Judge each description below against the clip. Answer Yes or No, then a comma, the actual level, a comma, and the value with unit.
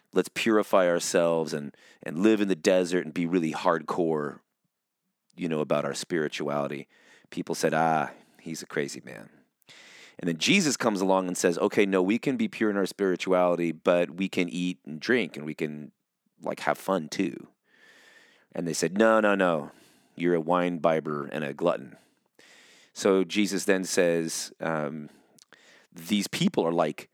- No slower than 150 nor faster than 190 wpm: Yes, average, 170 wpm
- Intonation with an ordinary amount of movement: Yes, average, 3.2 semitones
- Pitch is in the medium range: No, very low, 90 Hz